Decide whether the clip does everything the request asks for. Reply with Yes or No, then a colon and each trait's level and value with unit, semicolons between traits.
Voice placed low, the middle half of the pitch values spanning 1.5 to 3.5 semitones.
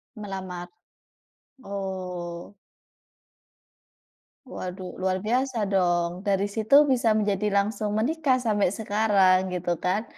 No: high, 200 Hz; average, 2.9 semitones